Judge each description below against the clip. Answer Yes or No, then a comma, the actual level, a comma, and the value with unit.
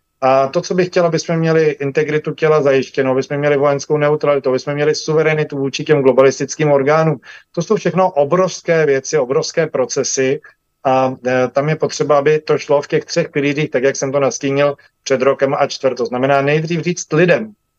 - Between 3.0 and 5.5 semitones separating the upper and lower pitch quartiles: No, narrow, 2.6 semitones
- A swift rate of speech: Yes, fast, 180 wpm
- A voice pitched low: No, medium, 145 Hz